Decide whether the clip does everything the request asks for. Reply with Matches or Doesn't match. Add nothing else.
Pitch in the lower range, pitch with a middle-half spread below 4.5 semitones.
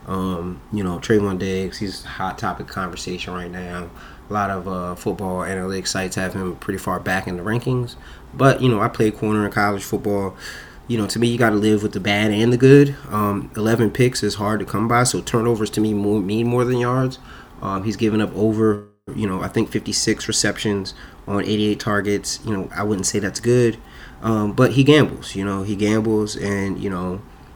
Matches